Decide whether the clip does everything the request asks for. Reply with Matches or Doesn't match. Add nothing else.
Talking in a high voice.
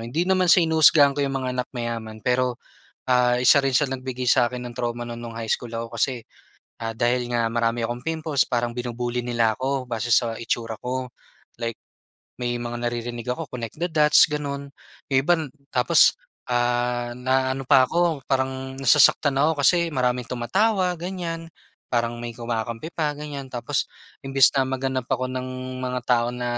Doesn't match